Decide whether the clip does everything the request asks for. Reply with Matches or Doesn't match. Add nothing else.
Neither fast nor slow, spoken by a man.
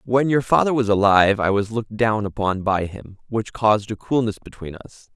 Doesn't match